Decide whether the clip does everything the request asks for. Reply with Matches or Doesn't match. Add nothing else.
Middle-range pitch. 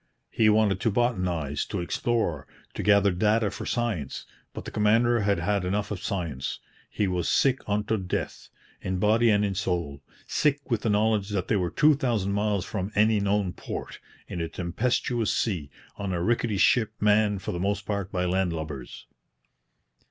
Doesn't match